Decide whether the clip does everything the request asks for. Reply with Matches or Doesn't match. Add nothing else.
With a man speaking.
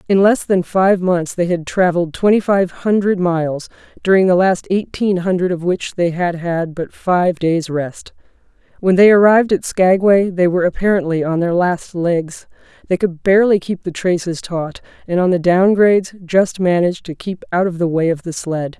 Doesn't match